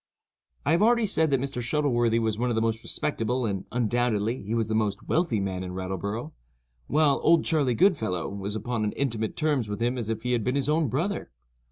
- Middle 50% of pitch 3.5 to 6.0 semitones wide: Yes, average, 4.9 semitones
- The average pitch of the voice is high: No, low, 120 Hz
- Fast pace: Yes, fast, 215 wpm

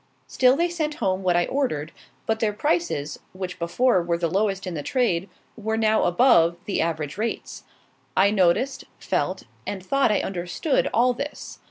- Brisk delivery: No, average, 170 wpm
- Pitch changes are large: Yes, wide, 6.4 semitones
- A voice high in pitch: Yes, high, 200 Hz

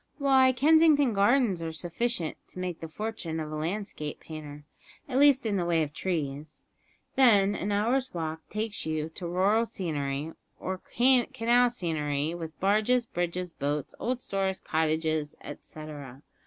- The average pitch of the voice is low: No, medium, 180 Hz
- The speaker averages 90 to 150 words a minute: Yes, average, 145 wpm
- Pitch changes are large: Yes, wide, 6.8 semitones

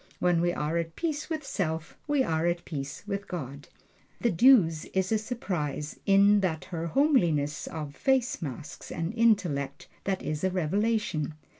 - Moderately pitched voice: Yes, medium, 175 Hz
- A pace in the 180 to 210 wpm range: No, average, 160 wpm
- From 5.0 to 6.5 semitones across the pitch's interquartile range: Yes, wide, 5.5 semitones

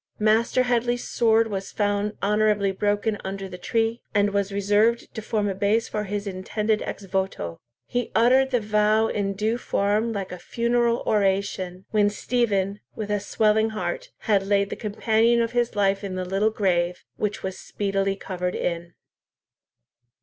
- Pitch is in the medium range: No, high, 205 Hz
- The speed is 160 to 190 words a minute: Yes, average, 165 wpm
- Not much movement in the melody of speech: Yes, narrow, 2.2 semitones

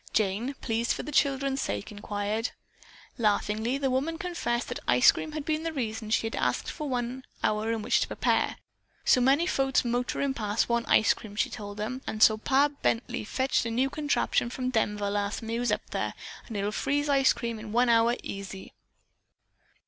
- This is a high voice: Yes, high, 235 Hz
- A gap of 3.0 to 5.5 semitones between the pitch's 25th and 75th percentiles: Yes, average, 3.9 semitones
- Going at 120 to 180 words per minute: No, average, 195 wpm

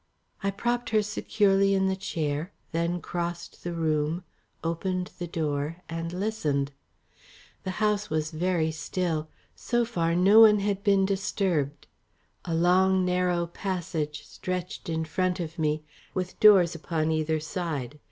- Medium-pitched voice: Yes, medium, 175 Hz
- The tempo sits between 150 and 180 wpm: No, average, 140 wpm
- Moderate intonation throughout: Yes, average, 3.3 semitones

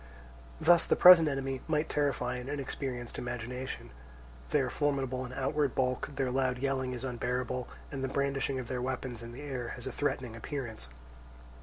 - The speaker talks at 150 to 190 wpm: Yes, average, 170 wpm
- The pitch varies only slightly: Yes, narrow, 1.8 semitones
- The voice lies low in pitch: Yes, low, 130 Hz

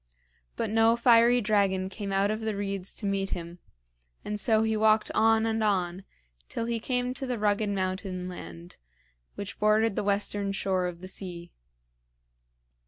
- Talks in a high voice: Yes, high, 205 Hz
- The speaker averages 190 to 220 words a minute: No, average, 165 wpm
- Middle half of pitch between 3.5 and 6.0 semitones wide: No, average, 2.8 semitones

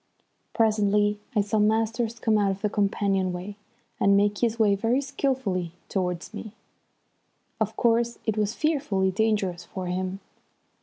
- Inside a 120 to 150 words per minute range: Yes, average, 145 wpm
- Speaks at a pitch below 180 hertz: No, high, 205 Hz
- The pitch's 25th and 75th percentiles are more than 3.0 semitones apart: No, narrow, 2.6 semitones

